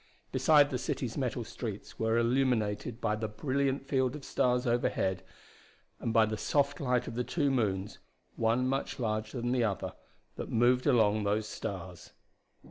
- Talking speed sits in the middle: Yes, average, 160 wpm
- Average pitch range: Yes, average, 3.2 semitones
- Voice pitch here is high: No, low, 120 Hz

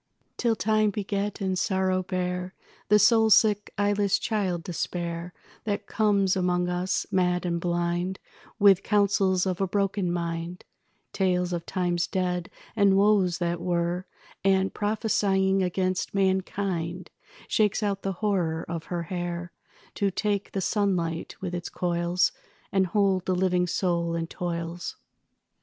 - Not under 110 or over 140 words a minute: Yes, slow, 135 wpm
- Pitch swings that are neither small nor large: No, narrow, 2.3 semitones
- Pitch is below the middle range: No, medium, 185 Hz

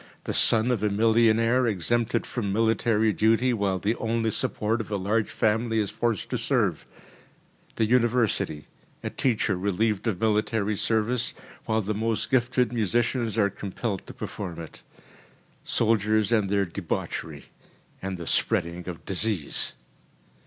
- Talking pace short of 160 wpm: Yes, average, 140 wpm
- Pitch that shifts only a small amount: Yes, narrow, 2.3 semitones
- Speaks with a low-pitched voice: Yes, low, 110 Hz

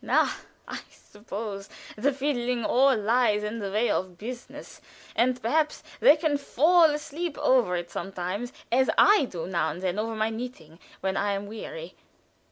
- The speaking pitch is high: Yes, high, 230 Hz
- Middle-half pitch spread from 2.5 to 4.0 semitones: No, wide, 5.6 semitones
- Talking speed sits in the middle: Yes, average, 160 wpm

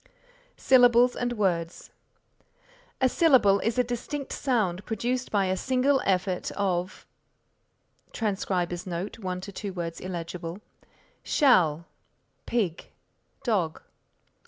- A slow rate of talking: Yes, slow, 100 wpm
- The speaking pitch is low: No, high, 200 Hz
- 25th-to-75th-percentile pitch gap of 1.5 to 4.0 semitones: No, wide, 5.4 semitones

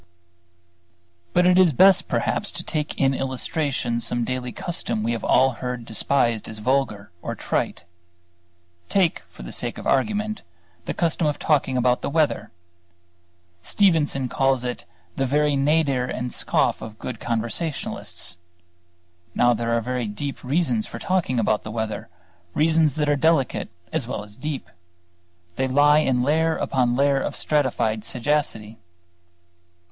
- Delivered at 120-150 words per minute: Yes, average, 145 wpm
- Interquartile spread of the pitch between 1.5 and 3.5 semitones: No, average, 4.2 semitones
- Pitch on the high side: No, low, 130 Hz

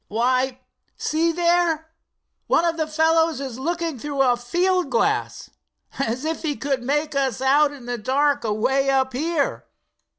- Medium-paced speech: Yes, average, 155 wpm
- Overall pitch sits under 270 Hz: No, very high, 285 Hz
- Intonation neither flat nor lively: Yes, average, 3.8 semitones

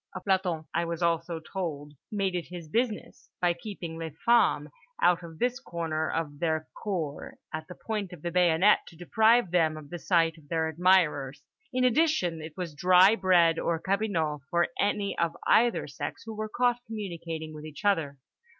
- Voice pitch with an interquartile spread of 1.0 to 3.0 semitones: No, average, 3.8 semitones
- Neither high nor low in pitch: Yes, medium, 170 Hz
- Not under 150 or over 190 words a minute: Yes, average, 180 wpm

